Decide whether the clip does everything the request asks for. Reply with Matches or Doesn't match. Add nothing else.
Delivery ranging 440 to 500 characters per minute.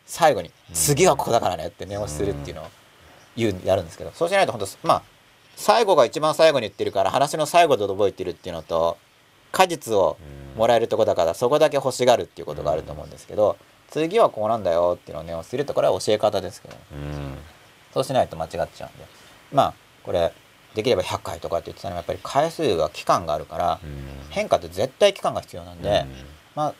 Matches